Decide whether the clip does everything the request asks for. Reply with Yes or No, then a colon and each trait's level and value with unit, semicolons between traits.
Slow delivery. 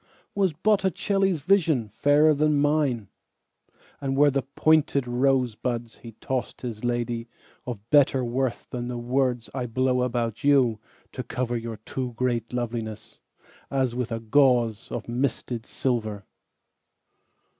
Yes: slow, 100 wpm